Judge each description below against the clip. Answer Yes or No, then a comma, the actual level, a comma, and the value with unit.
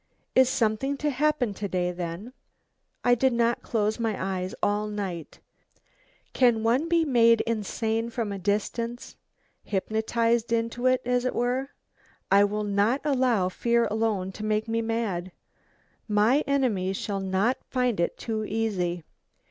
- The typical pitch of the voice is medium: No, high, 225 Hz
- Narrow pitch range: No, average, 3.3 semitones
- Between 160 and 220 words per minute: No, average, 145 wpm